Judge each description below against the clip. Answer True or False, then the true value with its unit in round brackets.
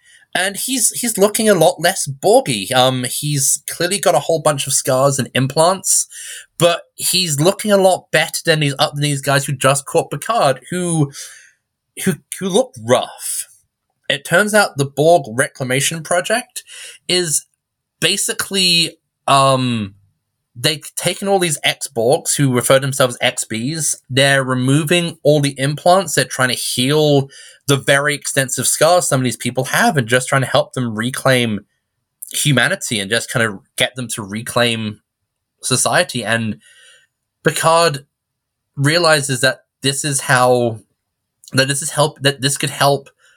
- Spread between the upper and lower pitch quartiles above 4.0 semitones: True (4.6 semitones)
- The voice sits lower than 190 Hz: True (140 Hz)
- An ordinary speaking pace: True (155 wpm)